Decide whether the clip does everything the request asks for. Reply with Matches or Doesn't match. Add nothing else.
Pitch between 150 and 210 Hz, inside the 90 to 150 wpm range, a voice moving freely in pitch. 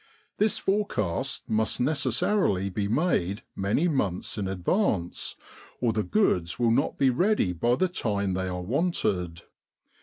Doesn't match